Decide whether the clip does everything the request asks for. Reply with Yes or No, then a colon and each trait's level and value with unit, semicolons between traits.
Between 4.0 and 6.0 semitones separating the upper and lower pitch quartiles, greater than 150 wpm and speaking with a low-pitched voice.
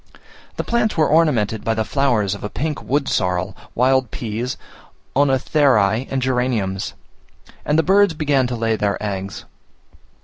No: average, 5.3 semitones; average, 145 wpm; low, 125 Hz